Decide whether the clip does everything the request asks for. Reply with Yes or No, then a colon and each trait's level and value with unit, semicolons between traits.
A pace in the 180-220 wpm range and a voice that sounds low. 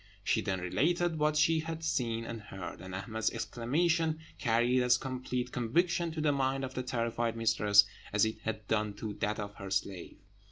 Yes: average, 185 wpm; low, 120 Hz